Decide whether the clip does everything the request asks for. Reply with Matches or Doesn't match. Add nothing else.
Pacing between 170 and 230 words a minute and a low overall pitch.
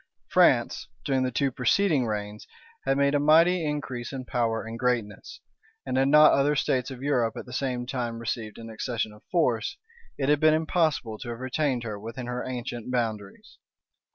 Matches